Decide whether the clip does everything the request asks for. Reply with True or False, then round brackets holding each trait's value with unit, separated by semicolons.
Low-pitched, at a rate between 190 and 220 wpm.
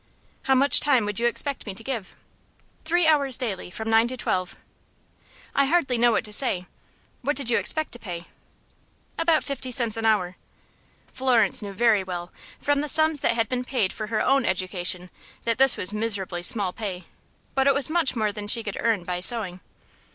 False (230 Hz; 195 wpm)